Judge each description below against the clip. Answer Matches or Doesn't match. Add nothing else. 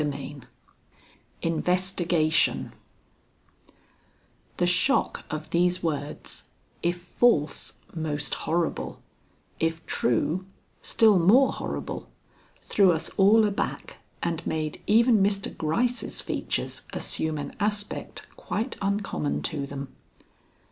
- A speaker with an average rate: Doesn't match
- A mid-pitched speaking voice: Matches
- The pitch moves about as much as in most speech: Matches